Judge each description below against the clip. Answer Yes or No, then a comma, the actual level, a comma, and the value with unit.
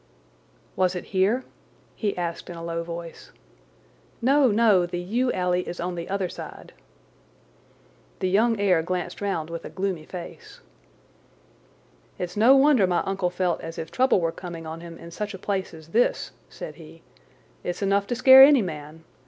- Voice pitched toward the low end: No, medium, 185 Hz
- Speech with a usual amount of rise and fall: Yes, average, 3.6 semitones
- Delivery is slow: No, average, 170 wpm